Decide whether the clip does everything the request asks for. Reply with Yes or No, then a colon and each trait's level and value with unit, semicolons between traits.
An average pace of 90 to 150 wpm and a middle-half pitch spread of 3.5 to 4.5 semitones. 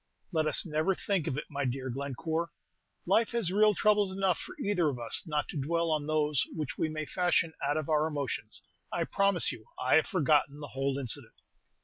No: fast, 205 wpm; average, 3.9 semitones